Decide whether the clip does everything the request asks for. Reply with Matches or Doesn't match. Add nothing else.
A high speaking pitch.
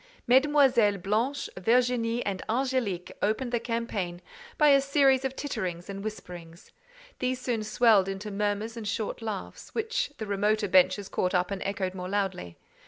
Matches